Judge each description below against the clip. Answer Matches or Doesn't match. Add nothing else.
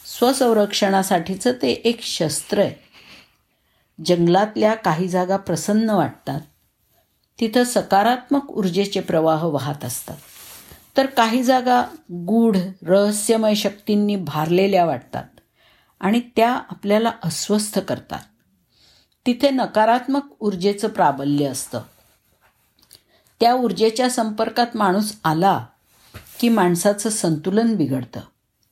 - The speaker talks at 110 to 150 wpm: Doesn't match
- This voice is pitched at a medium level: Doesn't match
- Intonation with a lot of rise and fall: Doesn't match